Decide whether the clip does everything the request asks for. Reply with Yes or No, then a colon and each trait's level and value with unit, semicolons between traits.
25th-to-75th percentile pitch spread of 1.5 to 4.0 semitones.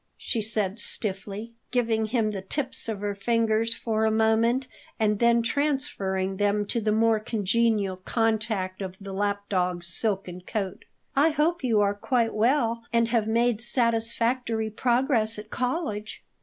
Yes: narrow, 2.4 semitones